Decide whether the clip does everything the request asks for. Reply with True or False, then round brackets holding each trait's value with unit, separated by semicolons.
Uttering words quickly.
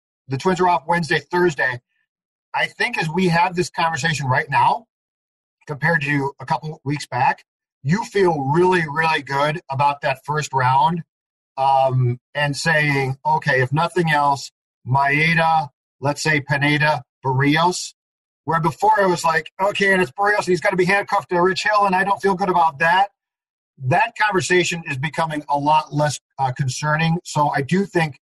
False (170 wpm)